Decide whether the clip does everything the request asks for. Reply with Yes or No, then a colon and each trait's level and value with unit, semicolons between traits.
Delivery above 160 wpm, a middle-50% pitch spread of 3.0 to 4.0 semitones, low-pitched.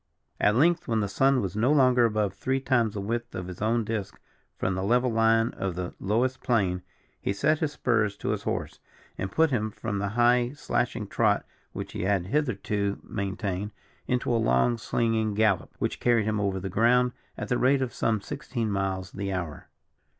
Yes: average, 195 wpm; average, 3.6 semitones; low, 110 Hz